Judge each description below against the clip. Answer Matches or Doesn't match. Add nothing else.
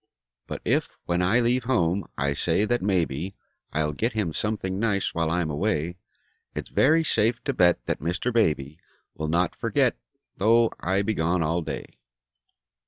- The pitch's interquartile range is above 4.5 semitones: Matches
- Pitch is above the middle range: Doesn't match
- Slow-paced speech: Doesn't match